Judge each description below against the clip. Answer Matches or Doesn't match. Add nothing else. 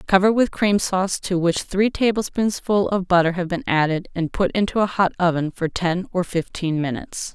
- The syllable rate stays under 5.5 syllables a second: Matches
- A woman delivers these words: Matches